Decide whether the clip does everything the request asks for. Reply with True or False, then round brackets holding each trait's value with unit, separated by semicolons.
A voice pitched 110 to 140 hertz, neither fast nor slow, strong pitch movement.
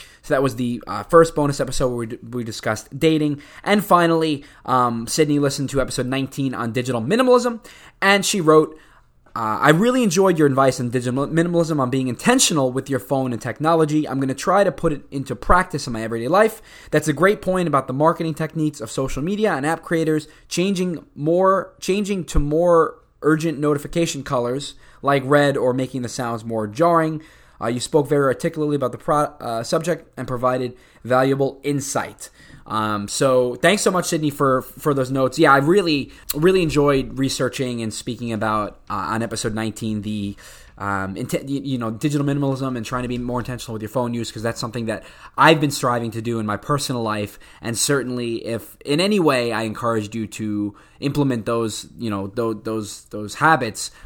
False (135 Hz; 190 wpm; 5.0 semitones)